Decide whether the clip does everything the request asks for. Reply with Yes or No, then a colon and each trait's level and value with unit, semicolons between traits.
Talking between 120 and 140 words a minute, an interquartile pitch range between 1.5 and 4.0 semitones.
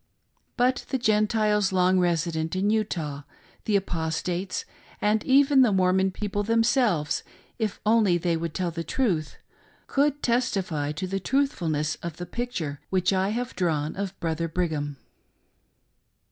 No: slow, 135 wpm; average, 4.8 semitones